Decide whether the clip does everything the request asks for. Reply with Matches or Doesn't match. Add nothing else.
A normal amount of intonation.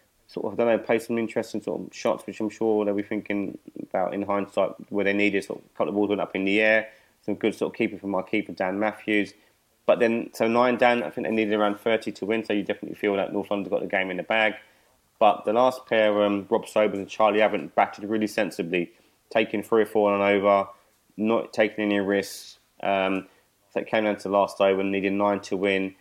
Doesn't match